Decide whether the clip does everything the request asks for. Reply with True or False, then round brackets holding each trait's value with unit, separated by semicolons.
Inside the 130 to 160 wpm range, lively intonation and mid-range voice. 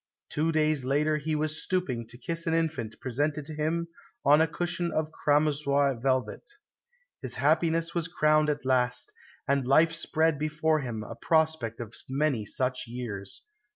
False (155 wpm; 3.6 semitones; 150 Hz)